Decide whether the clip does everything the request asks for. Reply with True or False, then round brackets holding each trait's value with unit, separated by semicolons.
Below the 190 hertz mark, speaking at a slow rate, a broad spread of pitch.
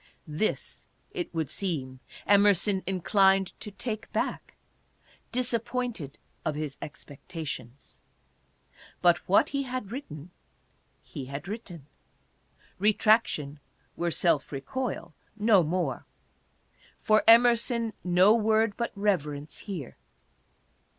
False (195 Hz; 100 wpm; 6.6 semitones)